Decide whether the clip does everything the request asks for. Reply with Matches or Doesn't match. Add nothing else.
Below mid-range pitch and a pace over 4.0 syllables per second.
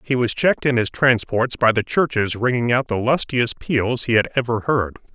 Matches